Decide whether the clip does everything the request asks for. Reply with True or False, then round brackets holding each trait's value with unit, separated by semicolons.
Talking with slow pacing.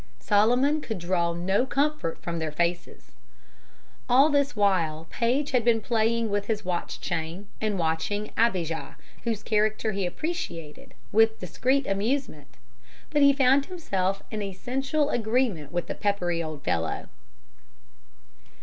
True (130 wpm)